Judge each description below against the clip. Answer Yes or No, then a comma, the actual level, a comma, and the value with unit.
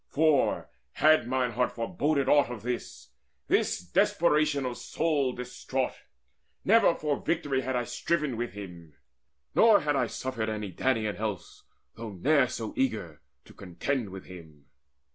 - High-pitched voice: No, low, 125 Hz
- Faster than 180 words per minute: No, average, 145 wpm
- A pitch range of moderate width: No, wide, 5.7 semitones